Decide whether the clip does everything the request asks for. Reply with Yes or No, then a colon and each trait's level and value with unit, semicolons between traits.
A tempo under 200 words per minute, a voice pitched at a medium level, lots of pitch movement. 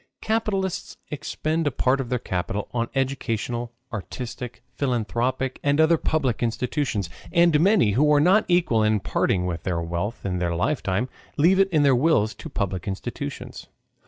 No: average, 160 wpm; low, 125 Hz; wide, 6.4 semitones